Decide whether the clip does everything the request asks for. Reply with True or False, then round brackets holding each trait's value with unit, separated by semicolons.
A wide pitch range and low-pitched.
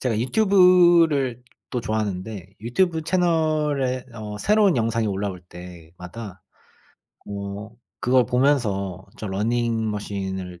True (6.5 semitones; 115 Hz)